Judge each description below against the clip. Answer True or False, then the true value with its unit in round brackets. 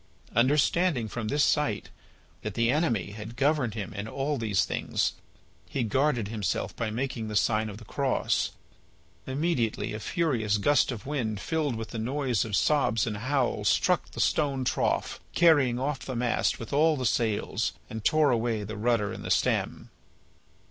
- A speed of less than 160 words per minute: False (170 wpm)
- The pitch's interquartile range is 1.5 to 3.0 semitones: False (4.6 semitones)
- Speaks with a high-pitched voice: False (120 Hz)